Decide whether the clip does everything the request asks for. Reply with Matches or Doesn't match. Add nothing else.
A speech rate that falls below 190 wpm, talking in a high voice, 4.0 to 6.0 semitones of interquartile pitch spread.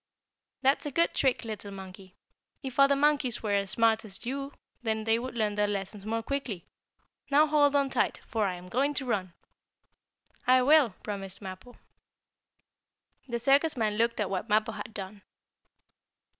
Matches